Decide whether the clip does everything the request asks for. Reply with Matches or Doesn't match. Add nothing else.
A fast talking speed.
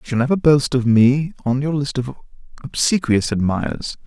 Doesn't match